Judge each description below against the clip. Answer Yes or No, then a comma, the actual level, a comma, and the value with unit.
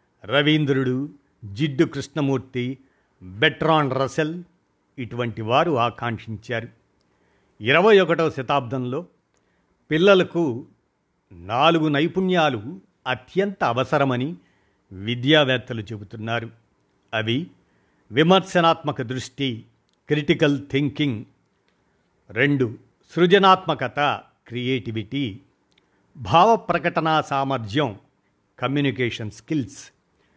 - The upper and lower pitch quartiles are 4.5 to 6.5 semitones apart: Yes, average, 4.9 semitones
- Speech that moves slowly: Yes, slow, 60 wpm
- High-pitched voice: No, low, 135 Hz